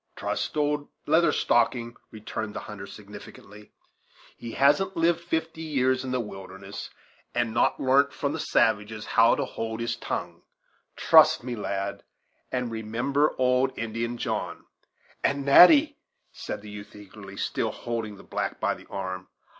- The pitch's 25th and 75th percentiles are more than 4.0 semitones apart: Yes, average, 5.1 semitones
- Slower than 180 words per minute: Yes, average, 150 wpm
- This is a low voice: Yes, low, 120 Hz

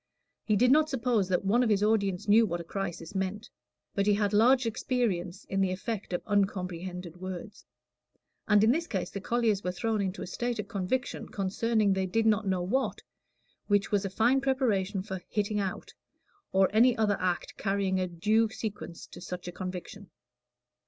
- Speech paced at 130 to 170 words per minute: No, average, 185 wpm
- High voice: Yes, high, 200 Hz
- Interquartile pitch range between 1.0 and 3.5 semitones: Yes, average, 3.0 semitones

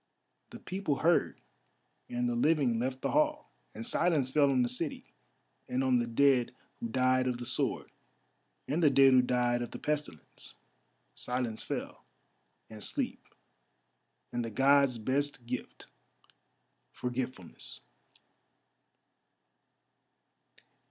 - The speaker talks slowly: Yes, slow, 120 wpm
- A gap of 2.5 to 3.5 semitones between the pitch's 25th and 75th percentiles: Yes, average, 2.8 semitones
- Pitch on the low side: Yes, low, 130 Hz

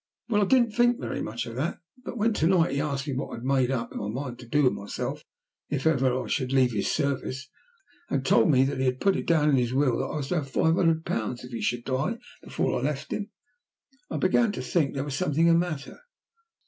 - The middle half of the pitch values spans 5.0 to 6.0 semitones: No, average, 4.3 semitones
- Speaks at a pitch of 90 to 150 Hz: Yes, medium, 140 Hz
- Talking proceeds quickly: Yes, fast, 250 wpm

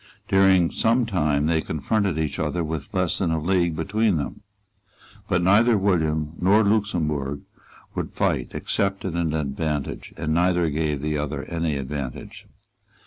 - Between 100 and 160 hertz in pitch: No, very low, 80 Hz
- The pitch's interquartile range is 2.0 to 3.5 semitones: No, average, 4.0 semitones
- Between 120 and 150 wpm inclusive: Yes, average, 145 wpm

